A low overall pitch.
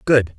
Yes: low, 115 Hz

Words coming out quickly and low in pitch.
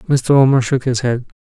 Yes: fast, 210 wpm; low, 130 Hz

